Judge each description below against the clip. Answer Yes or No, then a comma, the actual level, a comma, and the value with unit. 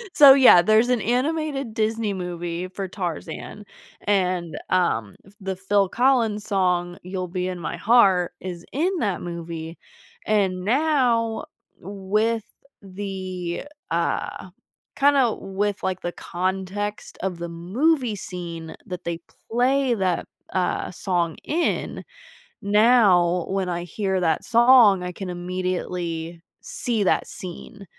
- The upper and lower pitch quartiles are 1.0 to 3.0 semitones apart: No, average, 4.1 semitones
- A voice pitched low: No, high, 190 Hz